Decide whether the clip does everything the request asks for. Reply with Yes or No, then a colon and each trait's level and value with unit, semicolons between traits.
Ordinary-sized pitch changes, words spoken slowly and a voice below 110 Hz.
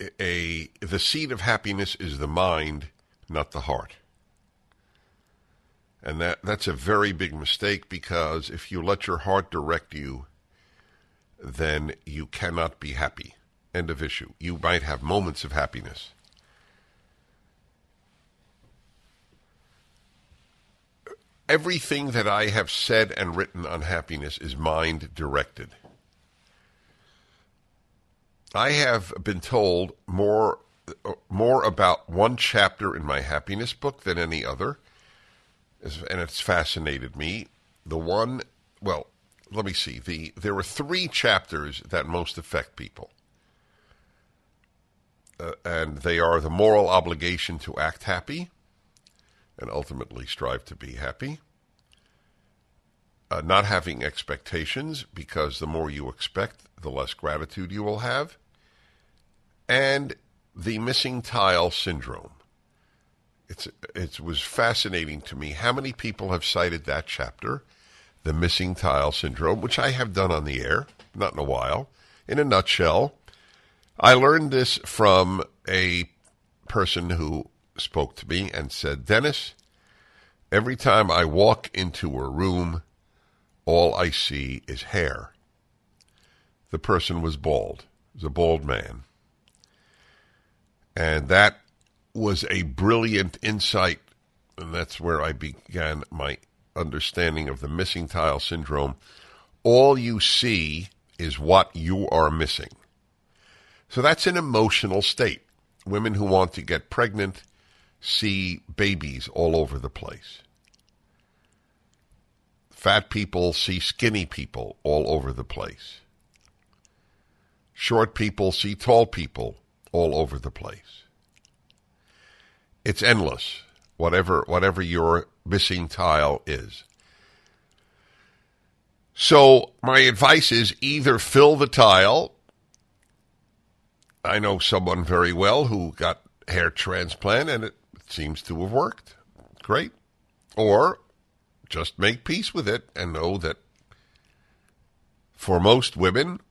Yes: average, 4.7 semitones; slow, 120 wpm; very low, 90 Hz